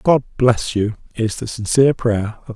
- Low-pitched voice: Yes, low, 115 Hz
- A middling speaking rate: Yes, average, 190 wpm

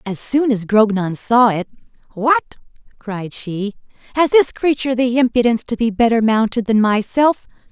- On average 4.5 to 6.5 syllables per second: Yes, 4.8 syllables/s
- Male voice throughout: No, female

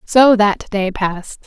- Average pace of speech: Yes, average, 165 wpm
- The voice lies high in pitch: Yes, high, 210 Hz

